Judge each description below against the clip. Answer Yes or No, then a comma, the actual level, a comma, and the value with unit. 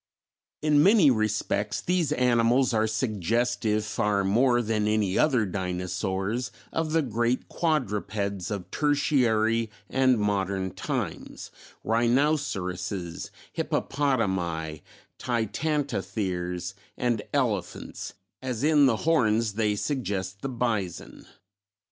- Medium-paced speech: No, slow, 95 wpm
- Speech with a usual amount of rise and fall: Yes, average, 4.7 semitones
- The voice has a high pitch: No, low, 110 Hz